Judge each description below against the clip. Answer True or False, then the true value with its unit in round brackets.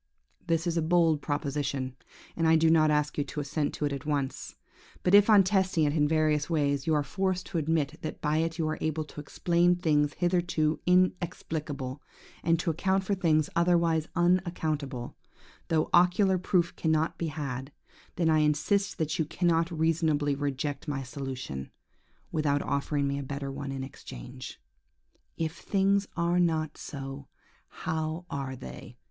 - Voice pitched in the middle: True (155 Hz)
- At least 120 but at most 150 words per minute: False (165 wpm)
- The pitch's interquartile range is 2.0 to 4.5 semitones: True (3.0 semitones)